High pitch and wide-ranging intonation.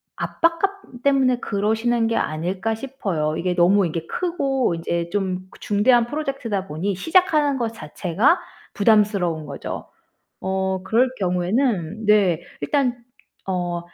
Yes: high, 210 Hz; wide, 6.1 semitones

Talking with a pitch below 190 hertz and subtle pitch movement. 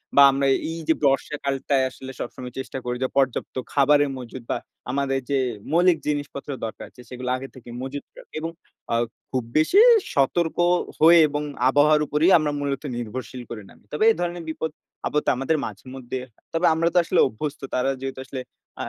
No: medium, 140 Hz; average, 3.0 semitones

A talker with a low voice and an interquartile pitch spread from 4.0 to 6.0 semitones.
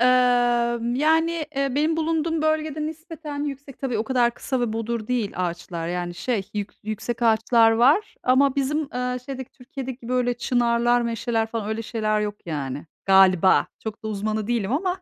No: high, 240 Hz; average, 4.5 semitones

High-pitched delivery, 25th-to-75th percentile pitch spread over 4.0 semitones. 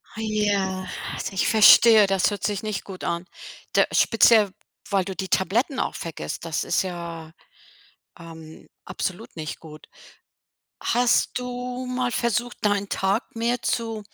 Yes: high, 200 Hz; average, 4.4 semitones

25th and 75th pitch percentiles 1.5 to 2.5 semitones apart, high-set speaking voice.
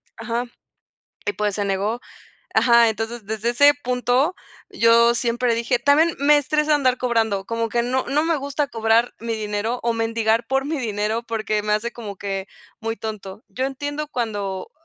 No: average, 2.9 semitones; high, 235 Hz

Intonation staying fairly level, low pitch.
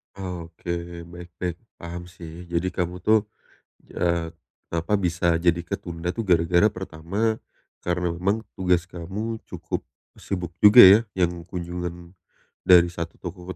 Yes: narrow, 1.4 semitones; very low, 90 Hz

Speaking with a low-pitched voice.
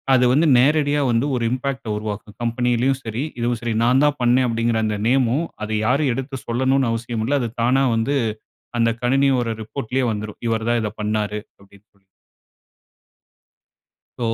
Yes: low, 120 Hz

